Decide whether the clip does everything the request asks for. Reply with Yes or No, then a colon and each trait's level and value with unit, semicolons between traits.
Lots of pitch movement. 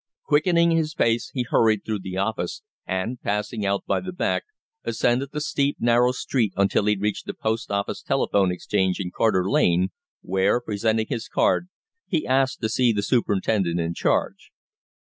No: average, 4.3 semitones